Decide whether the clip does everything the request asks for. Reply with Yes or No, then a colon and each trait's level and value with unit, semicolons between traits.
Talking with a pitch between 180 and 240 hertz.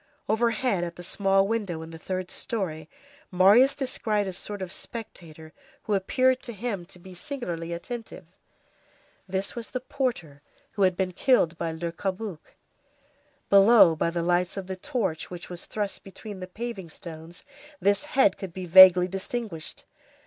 Yes: high, 190 Hz